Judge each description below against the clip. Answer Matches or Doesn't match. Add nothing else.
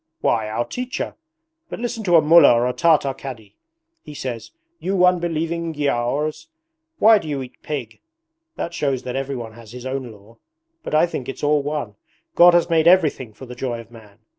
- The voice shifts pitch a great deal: Matches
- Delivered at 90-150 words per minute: Doesn't match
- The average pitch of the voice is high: Doesn't match